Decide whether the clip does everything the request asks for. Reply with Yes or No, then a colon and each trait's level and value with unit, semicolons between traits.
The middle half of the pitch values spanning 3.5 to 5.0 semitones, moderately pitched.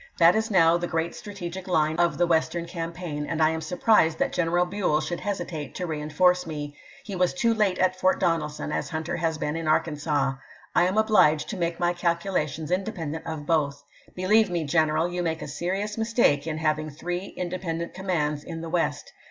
No: average, 2.7 semitones; medium, 170 Hz